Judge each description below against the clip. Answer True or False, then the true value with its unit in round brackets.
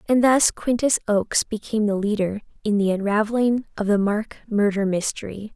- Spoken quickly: False (160 wpm)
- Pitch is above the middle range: True (210 Hz)